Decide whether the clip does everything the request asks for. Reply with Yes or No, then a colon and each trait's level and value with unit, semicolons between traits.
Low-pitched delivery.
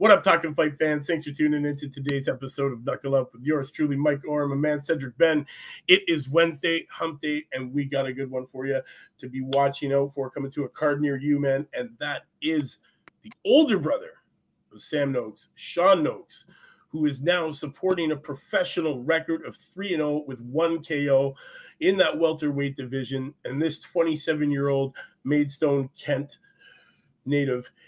No: medium, 145 Hz